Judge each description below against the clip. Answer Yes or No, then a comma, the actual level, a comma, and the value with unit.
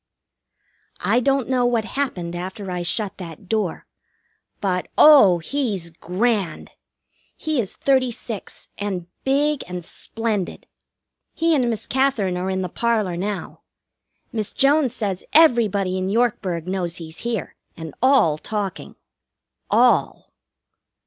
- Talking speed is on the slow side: Yes, slow, 125 wpm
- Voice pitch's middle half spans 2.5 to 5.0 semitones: No, wide, 5.4 semitones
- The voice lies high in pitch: Yes, high, 205 Hz